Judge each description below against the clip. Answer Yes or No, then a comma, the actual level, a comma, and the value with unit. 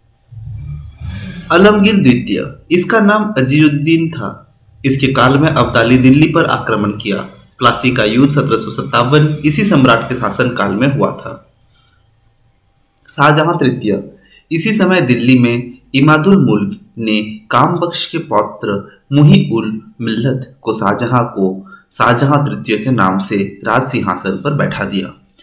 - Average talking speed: No, slow, 125 wpm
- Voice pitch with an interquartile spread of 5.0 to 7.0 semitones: Yes, wide, 5.4 semitones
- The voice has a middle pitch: No, low, 125 Hz